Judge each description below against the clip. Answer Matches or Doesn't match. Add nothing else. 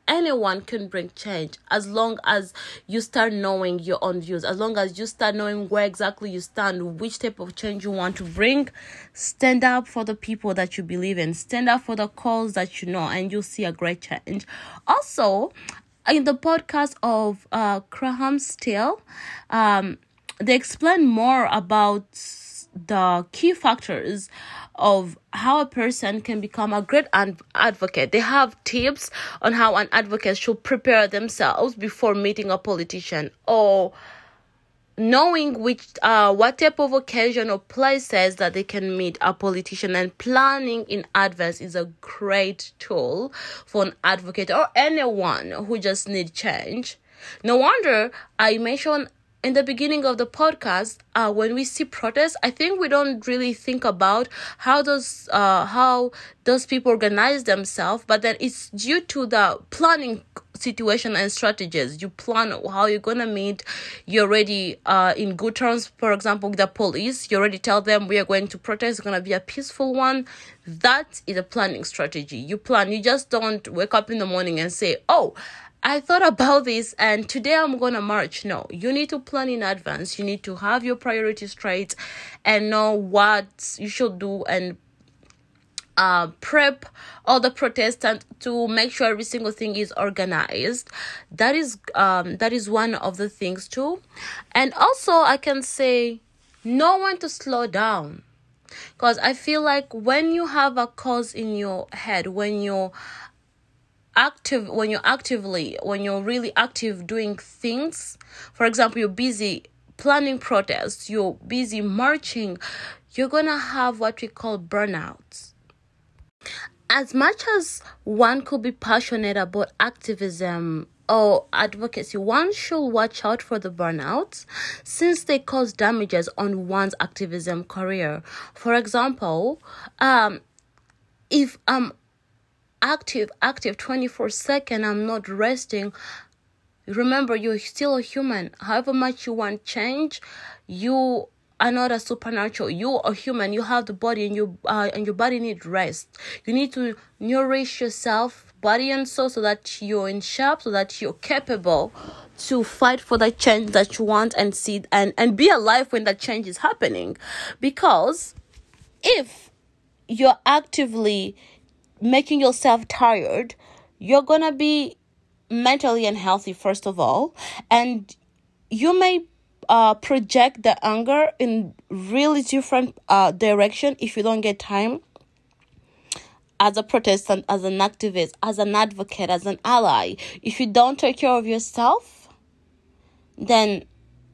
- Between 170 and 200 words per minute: Doesn't match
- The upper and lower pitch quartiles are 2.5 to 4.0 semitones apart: Doesn't match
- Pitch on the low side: Doesn't match